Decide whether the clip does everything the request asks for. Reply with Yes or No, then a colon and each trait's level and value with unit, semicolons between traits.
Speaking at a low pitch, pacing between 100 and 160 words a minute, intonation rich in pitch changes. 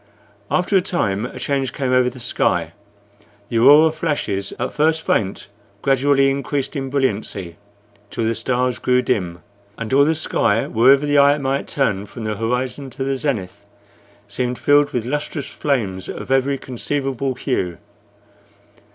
No: low, 130 Hz; average, 150 wpm; average, 3.7 semitones